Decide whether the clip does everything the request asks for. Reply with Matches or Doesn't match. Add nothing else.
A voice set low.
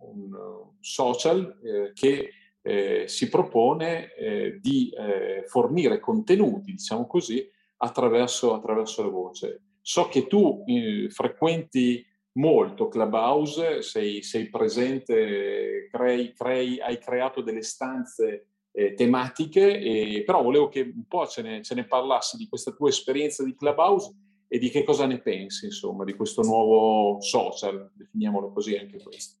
Doesn't match